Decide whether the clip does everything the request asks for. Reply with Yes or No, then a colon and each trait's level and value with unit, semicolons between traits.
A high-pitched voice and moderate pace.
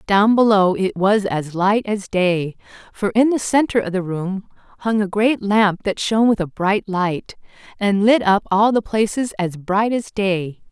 Yes: high, 200 Hz; average, 195 wpm